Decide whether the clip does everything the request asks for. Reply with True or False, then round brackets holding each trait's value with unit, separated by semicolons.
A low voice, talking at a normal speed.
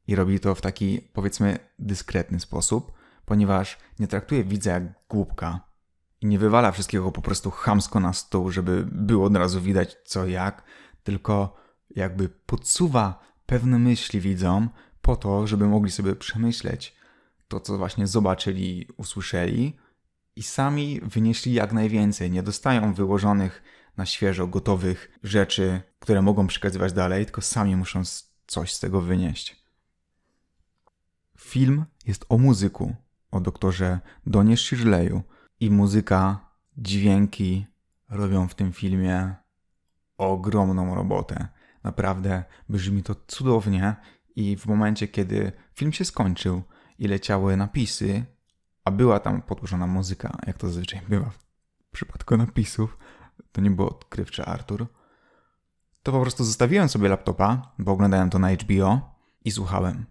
True (100 Hz; 130 wpm)